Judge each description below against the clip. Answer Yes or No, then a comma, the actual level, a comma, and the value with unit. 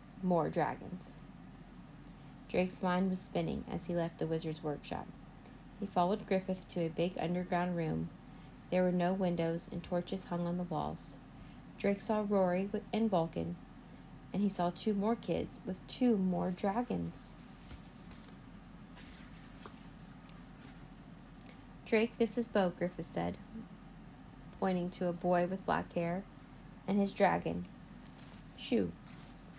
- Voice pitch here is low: No, medium, 180 Hz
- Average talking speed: No, slow, 125 wpm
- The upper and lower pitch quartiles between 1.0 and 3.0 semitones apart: Yes, narrow, 2.6 semitones